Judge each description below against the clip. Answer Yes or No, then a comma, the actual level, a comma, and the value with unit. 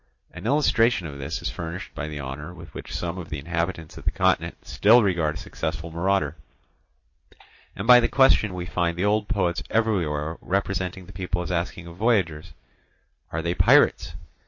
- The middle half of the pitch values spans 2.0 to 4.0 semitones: Yes, average, 3.4 semitones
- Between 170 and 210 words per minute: Yes, average, 175 wpm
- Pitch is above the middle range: No, very low, 90 Hz